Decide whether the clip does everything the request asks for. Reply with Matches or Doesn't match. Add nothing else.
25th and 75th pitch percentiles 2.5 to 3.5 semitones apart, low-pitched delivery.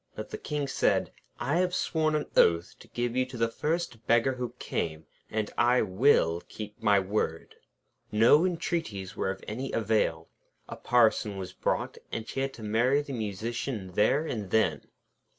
Doesn't match